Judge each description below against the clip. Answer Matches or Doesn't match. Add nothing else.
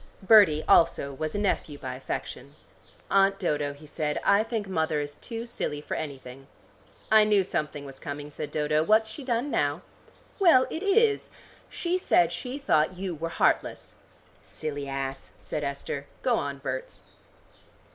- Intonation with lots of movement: Matches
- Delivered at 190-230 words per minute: Doesn't match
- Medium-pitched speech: Matches